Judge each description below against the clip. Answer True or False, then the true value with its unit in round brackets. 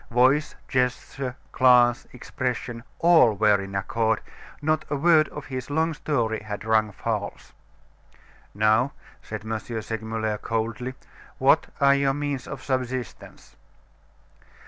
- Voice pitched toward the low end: True (125 Hz)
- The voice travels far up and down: False (3.9 semitones)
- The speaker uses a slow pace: True (120 wpm)